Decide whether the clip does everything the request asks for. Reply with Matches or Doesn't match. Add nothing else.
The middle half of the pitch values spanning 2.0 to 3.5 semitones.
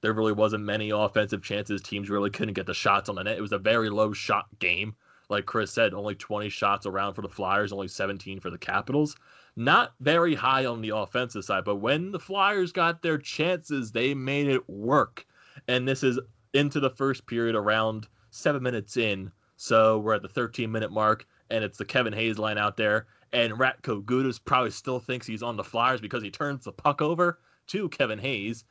Doesn't match